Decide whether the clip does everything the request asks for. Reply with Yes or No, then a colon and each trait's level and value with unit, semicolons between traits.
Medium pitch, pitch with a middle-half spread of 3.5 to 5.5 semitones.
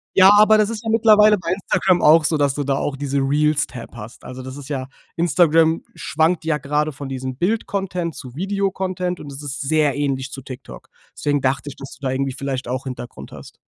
Yes: medium, 150 Hz; average, 4.8 semitones